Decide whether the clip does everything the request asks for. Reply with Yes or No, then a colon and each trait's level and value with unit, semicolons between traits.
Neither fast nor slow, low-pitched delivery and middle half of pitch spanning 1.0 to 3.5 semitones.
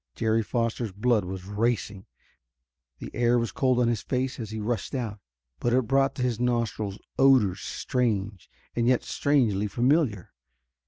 Yes: average, 155 wpm; low, 115 Hz; average, 3.1 semitones